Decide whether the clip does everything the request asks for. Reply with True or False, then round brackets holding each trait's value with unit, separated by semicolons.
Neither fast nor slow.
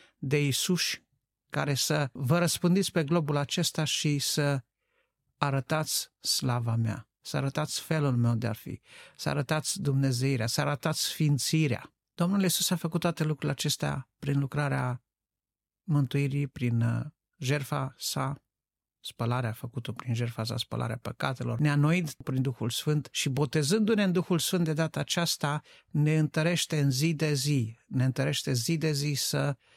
True (145 wpm)